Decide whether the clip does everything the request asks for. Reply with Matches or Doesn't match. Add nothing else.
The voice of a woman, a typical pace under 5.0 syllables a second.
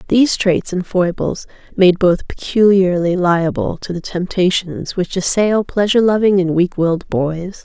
Matches